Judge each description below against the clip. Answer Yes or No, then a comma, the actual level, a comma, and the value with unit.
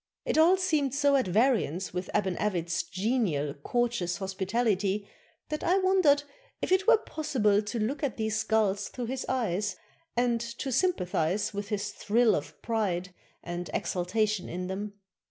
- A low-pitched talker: No, high, 215 Hz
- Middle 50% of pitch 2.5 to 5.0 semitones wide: No, wide, 5.5 semitones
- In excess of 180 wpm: No, average, 155 wpm